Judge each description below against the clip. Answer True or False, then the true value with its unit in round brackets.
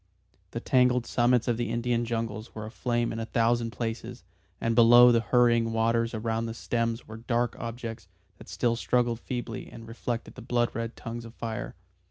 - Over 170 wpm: True (180 wpm)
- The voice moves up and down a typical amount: False (1.0 semitones)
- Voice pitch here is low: True (115 Hz)